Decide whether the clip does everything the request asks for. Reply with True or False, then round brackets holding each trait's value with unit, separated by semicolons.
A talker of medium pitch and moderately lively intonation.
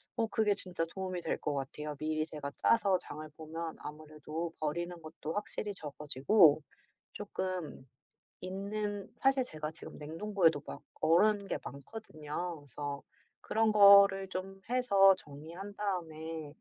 True (170 Hz; 4.5 semitones)